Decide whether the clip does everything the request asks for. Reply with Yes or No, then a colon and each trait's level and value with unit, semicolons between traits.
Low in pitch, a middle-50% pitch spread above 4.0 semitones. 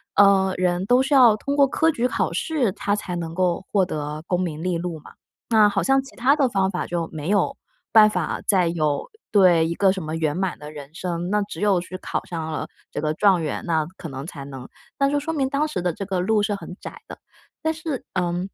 No: medium, 185 Hz; average, 4.5 semitones